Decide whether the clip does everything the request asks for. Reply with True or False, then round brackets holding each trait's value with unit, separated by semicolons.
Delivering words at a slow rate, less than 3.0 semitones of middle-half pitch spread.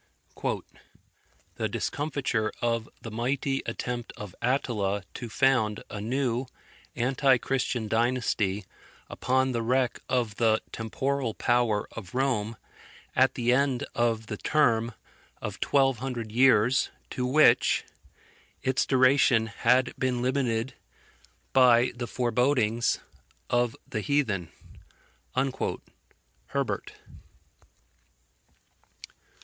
True (100 wpm; 2.6 semitones)